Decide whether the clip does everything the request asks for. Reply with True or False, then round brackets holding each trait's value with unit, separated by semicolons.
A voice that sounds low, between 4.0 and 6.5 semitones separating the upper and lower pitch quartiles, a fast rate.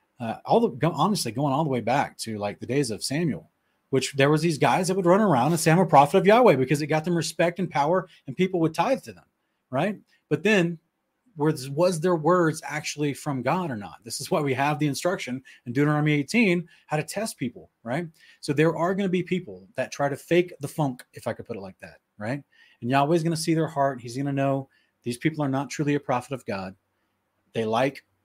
False (150 Hz; 4.4 semitones; 245 wpm)